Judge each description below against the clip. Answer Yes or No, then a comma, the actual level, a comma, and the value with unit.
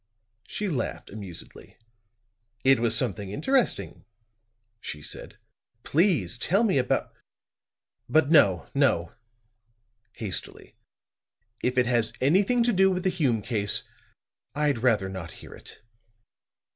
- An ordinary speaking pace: No, slow, 115 wpm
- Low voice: Yes, low, 125 Hz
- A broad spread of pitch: Yes, wide, 8.9 semitones